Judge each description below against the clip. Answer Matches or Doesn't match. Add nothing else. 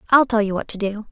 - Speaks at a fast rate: Matches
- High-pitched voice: Matches